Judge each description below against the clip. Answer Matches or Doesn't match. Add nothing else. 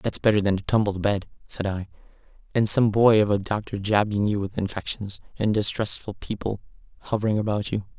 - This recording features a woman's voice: Doesn't match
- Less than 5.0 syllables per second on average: Doesn't match